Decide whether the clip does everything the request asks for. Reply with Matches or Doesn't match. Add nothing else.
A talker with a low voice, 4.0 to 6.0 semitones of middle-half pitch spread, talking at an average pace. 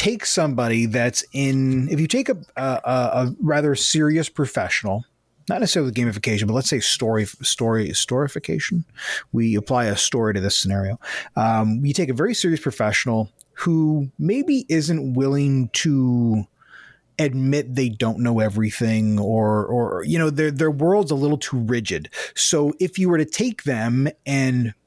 Matches